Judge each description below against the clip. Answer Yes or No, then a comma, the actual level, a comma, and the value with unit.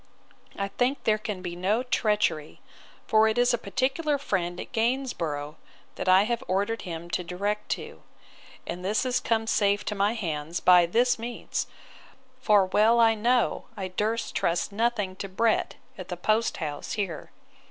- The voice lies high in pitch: Yes, high, 210 Hz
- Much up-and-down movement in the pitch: No, average, 4.2 semitones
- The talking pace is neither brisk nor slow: Yes, average, 165 wpm